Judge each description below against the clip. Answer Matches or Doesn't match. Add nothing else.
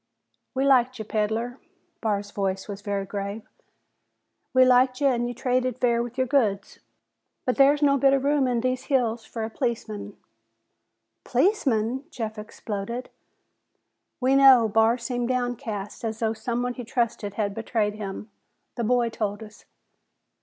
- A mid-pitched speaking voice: Doesn't match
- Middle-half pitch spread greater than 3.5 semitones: Doesn't match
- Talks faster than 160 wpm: Doesn't match